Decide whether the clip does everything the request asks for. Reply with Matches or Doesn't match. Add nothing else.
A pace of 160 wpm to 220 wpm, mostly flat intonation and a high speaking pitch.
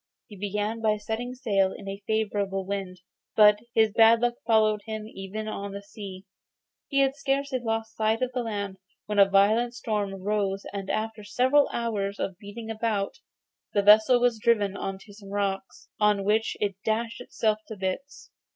Matches